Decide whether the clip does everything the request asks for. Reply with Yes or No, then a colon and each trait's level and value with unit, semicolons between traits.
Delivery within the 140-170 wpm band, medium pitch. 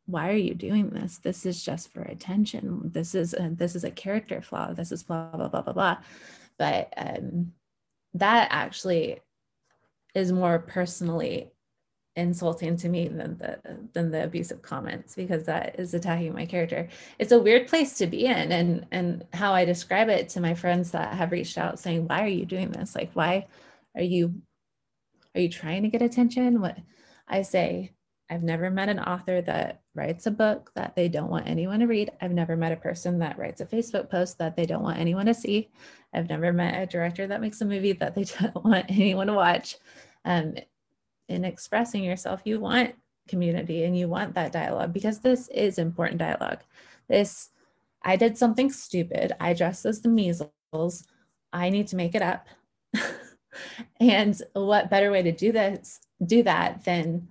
No: average, 185 wpm; medium, 180 Hz